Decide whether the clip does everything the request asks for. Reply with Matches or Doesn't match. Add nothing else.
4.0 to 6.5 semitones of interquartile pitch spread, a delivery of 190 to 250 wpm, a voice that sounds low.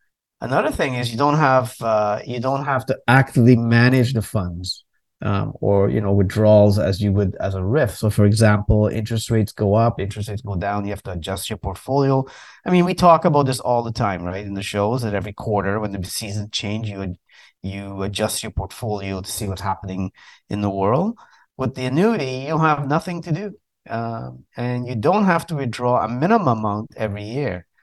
Matches